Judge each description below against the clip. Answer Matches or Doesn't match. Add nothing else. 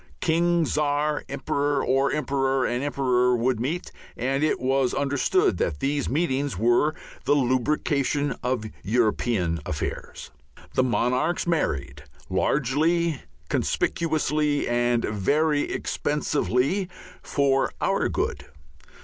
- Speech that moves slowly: Matches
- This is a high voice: Doesn't match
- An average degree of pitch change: Matches